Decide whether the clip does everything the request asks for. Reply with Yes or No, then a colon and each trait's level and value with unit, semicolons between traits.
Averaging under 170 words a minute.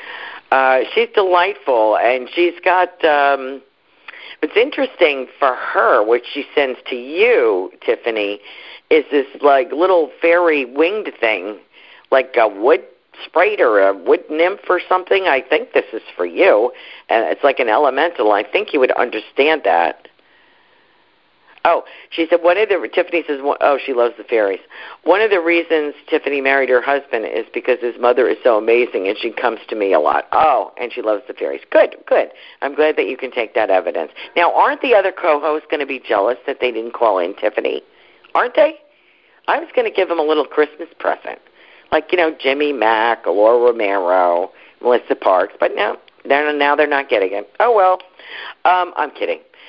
No: average, 180 wpm